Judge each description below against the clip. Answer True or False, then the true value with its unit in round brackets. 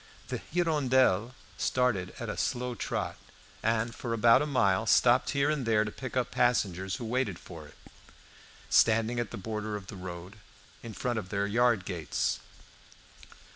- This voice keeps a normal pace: True (165 wpm)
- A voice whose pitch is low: True (115 Hz)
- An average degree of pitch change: True (3.9 semitones)